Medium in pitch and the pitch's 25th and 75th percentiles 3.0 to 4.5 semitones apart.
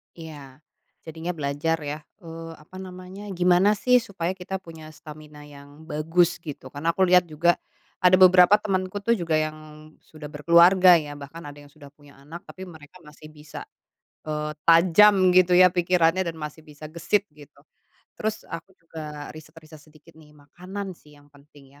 Yes: medium, 165 Hz; average, 3.3 semitones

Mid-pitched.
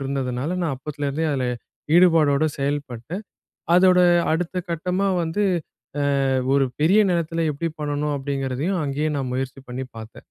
Yes: medium, 145 Hz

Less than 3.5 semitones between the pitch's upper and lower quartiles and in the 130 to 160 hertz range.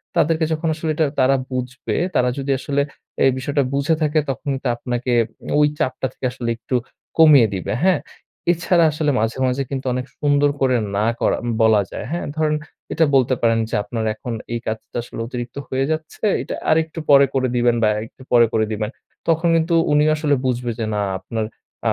No: average, 4.3 semitones; low, 135 Hz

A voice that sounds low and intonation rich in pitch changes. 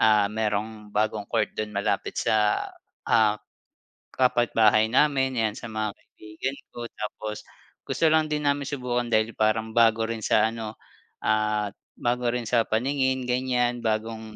No: low, 110 Hz; narrow, 2.4 semitones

